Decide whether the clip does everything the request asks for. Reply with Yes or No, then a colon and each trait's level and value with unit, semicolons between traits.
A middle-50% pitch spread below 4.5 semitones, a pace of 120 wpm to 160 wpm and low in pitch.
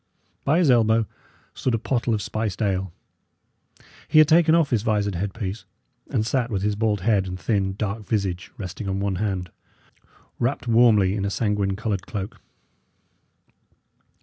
Yes: average, 3.0 semitones; average, 155 wpm; low, 105 Hz